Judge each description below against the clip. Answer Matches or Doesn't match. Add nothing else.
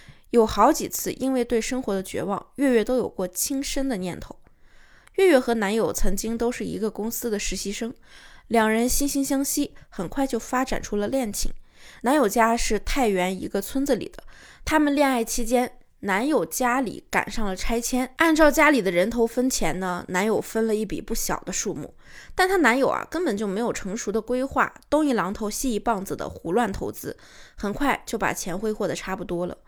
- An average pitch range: Matches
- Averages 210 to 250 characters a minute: Doesn't match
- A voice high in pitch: Matches